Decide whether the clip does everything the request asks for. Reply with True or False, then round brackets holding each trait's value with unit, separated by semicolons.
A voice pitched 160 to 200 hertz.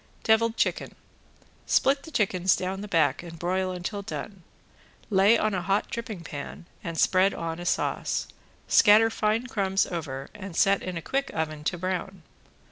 True (190 Hz)